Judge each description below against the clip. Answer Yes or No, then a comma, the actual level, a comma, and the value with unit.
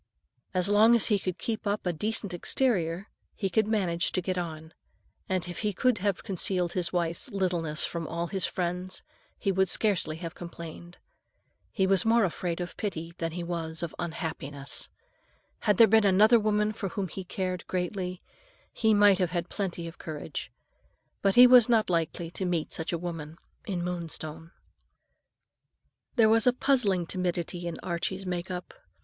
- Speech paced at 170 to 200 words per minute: Yes, average, 175 wpm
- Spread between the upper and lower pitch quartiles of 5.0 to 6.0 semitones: No, average, 3.2 semitones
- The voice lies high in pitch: No, medium, 180 Hz